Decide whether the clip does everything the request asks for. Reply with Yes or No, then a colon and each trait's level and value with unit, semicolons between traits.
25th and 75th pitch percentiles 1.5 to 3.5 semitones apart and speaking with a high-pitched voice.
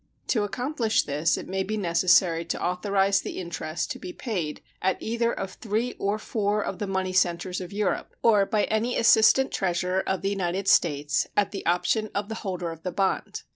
Yes: average, 3.0 semitones; high, 195 Hz